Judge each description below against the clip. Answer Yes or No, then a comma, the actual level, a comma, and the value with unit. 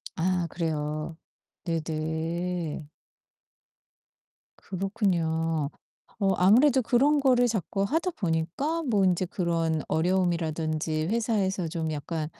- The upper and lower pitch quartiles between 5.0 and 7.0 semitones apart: No, average, 4.1 semitones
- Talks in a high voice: No, medium, 175 Hz